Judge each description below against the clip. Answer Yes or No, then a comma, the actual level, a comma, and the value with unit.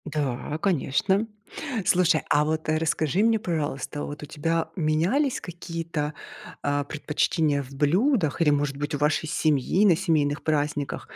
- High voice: No, medium, 155 Hz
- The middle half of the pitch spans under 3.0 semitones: Yes, narrow, 2.6 semitones